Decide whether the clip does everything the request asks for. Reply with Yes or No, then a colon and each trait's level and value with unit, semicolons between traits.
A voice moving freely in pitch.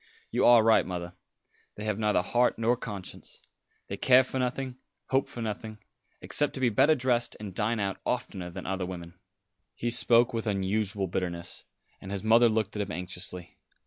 No: average, 4.1 semitones